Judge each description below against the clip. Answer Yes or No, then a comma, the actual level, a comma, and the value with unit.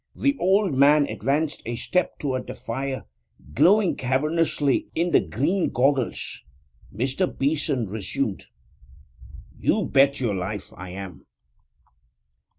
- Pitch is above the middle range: No, low, 135 Hz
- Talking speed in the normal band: No, slow, 115 wpm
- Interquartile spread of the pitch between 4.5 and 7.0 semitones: Yes, average, 5.2 semitones